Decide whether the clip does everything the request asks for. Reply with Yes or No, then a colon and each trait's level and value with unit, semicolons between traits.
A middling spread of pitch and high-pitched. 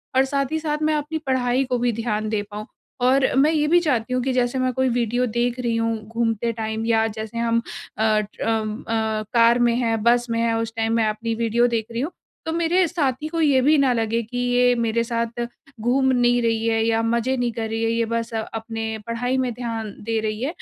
No: narrow, 2.3 semitones; high, 235 Hz